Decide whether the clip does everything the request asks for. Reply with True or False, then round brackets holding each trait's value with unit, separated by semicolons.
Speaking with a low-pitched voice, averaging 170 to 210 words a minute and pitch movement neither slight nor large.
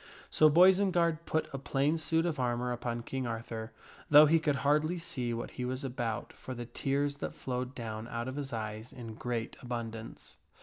True (130 Hz; 185 wpm; 4.2 semitones)